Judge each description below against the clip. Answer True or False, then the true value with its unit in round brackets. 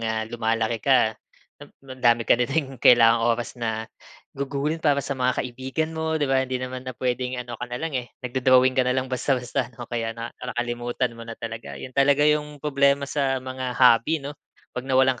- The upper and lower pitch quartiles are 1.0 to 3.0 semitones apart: True (2.4 semitones)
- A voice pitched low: True (130 Hz)